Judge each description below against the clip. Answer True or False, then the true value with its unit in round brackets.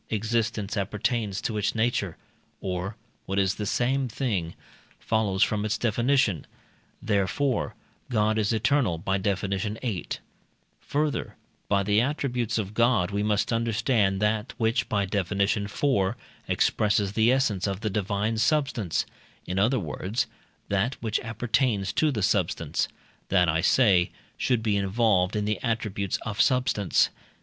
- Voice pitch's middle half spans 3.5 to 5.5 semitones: False (3.0 semitones)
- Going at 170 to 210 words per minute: False (135 wpm)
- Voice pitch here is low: True (105 Hz)